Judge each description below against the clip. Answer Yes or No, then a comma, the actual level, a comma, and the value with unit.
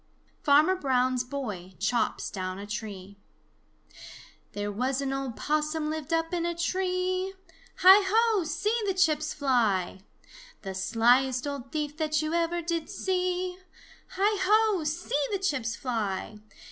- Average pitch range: No, wide, 7.0 semitones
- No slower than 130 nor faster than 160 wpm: Yes, average, 140 wpm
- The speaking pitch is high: Yes, very high, 300 Hz